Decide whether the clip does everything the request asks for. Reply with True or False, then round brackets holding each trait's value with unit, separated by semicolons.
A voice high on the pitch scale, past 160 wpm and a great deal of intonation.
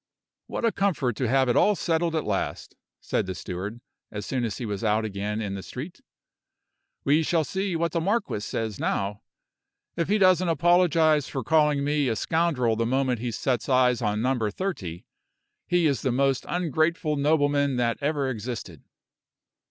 False (135 Hz; 175 wpm; 6.3 semitones)